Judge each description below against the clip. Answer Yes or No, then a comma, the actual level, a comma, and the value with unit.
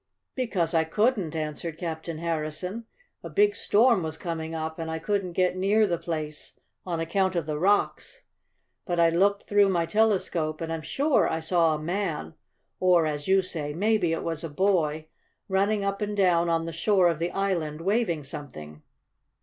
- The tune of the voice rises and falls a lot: No, average, 3.7 semitones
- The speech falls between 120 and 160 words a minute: No, average, 180 wpm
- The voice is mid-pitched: Yes, medium, 170 Hz